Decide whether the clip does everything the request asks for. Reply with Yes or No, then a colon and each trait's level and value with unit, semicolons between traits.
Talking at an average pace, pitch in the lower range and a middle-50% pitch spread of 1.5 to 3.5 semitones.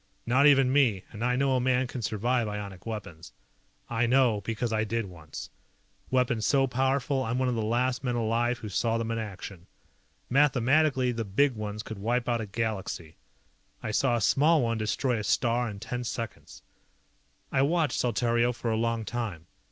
Yes: average, 185 wpm; low, 120 Hz; average, 2.9 semitones